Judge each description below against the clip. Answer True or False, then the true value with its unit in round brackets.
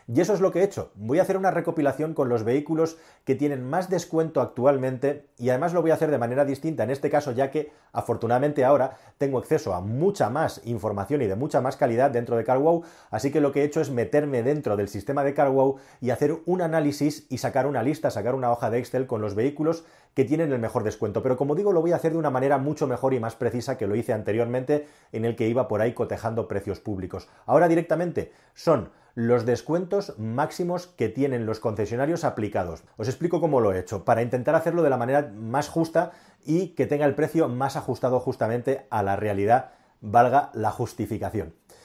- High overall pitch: False (135 Hz)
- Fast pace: True (215 wpm)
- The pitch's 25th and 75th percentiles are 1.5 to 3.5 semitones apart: False (4.5 semitones)